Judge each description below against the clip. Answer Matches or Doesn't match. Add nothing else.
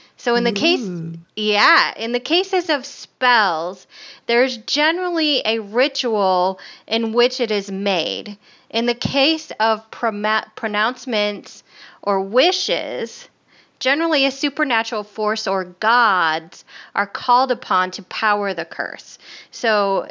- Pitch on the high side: Matches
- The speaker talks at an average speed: Doesn't match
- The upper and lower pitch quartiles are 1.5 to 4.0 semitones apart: Doesn't match